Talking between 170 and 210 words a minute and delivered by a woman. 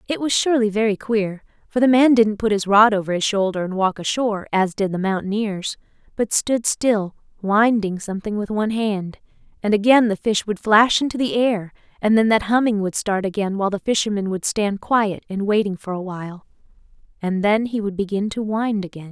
Yes: average, 200 wpm; female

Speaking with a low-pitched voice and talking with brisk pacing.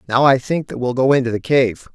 Yes: low, 130 Hz; fast, 280 wpm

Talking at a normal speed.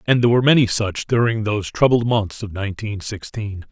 Yes: average, 195 wpm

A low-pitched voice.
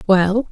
No: high, 200 Hz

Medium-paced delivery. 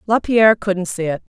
Yes: average, 180 wpm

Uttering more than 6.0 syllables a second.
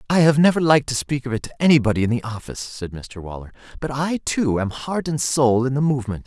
Yes: 6.3 syllables/s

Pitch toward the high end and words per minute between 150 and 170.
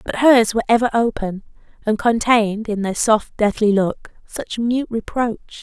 Yes: high, 220 Hz; average, 160 wpm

